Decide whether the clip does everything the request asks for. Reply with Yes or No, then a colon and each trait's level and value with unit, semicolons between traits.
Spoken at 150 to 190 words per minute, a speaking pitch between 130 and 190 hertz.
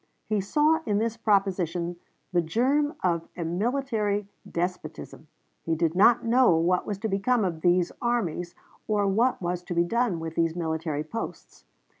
Yes: average, 160 wpm; medium, 185 Hz